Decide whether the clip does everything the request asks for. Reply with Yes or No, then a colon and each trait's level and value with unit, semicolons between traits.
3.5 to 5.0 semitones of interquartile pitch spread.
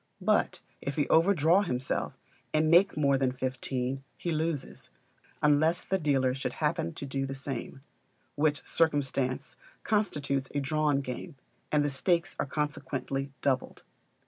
No: average, 2.8 semitones